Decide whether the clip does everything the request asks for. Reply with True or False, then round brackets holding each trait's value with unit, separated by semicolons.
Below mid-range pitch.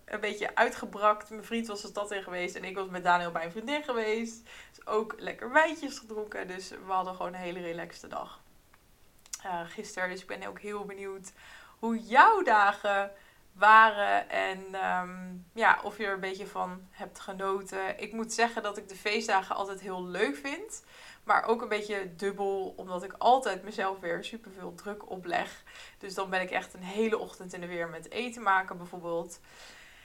False (200 Hz)